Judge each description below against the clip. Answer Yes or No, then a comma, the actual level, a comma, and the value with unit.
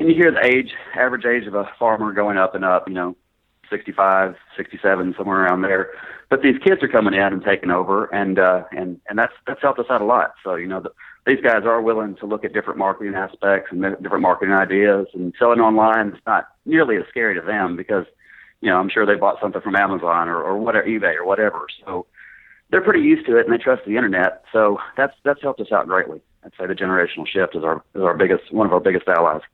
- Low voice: Yes, low, 100 Hz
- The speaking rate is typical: No, fast, 240 wpm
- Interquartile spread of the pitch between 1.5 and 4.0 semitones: Yes, average, 3.4 semitones